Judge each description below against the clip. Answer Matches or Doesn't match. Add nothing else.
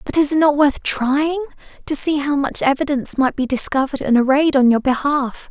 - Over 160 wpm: Matches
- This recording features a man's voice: Doesn't match